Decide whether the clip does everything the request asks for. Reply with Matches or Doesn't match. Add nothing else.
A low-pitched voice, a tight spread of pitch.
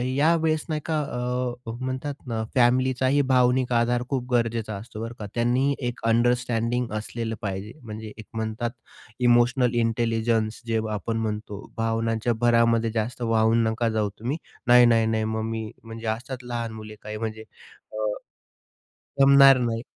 Matches